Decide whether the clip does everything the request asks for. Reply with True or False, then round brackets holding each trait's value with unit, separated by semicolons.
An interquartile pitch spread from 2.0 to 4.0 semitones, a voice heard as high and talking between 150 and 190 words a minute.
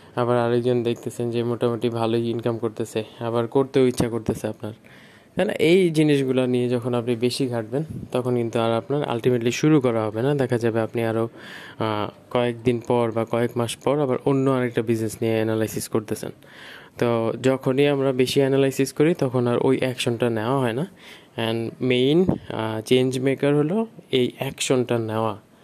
False (2.6 semitones; 120 Hz; 165 wpm)